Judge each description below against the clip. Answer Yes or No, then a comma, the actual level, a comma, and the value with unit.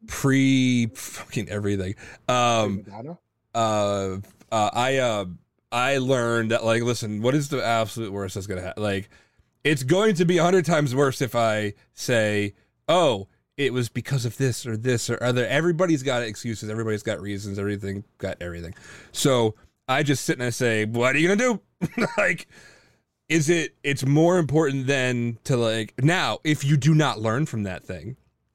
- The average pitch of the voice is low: Yes, low, 120 Hz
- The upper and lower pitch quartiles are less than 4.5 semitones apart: No, average, 4.9 semitones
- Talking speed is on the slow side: No, average, 170 wpm